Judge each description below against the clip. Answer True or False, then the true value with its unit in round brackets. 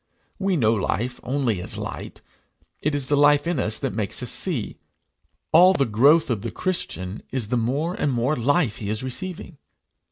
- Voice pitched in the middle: False (130 Hz)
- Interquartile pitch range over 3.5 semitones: True (5.3 semitones)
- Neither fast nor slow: True (185 wpm)